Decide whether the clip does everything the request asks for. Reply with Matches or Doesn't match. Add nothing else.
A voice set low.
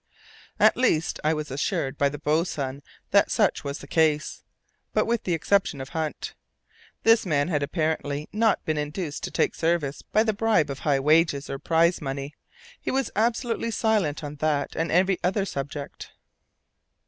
Doesn't match